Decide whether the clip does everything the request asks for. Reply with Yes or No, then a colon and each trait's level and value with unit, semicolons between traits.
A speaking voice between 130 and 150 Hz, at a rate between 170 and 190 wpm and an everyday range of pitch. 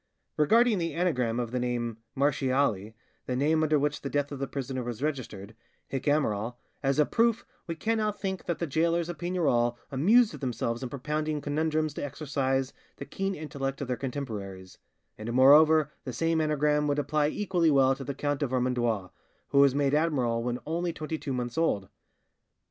Yes: medium, 140 Hz; average, 180 wpm; average, 3.9 semitones